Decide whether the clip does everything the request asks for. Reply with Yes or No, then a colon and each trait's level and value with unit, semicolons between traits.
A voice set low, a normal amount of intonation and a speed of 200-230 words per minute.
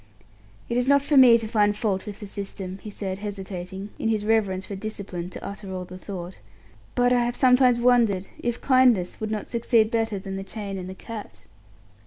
No: high, 210 Hz; average, 3.5 semitones; fast, 205 wpm